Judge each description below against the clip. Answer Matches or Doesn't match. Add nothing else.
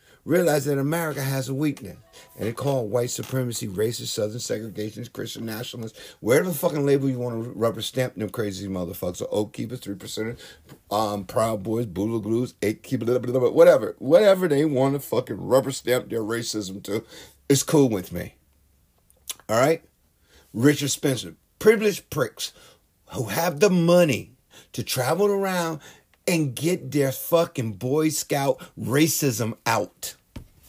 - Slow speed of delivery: Doesn't match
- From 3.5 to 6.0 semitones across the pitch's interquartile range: Matches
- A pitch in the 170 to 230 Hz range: Doesn't match